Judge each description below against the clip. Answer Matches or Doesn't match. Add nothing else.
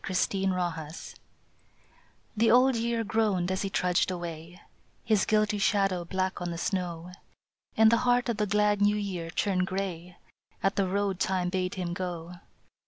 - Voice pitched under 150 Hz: Doesn't match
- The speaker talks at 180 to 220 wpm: Doesn't match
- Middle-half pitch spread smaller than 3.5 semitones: Matches